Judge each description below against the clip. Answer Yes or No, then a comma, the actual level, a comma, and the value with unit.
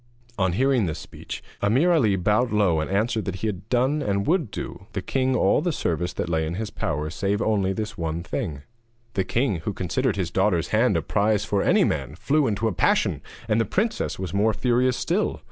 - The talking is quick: Yes, fast, 215 wpm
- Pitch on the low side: Yes, low, 105 Hz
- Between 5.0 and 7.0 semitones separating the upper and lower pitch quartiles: Yes, average, 5.3 semitones